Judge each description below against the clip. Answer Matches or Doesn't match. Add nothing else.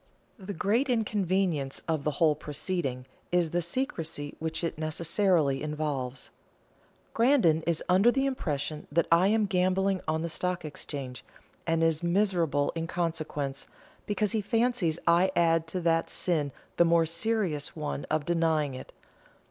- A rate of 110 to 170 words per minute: Matches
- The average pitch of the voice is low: Doesn't match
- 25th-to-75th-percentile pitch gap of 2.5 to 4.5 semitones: Matches